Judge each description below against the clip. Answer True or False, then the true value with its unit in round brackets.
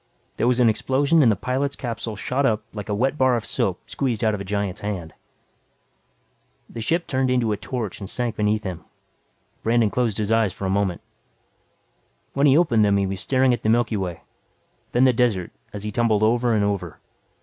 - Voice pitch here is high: False (110 Hz)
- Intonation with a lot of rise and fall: False (3.6 semitones)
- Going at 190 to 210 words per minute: True (205 wpm)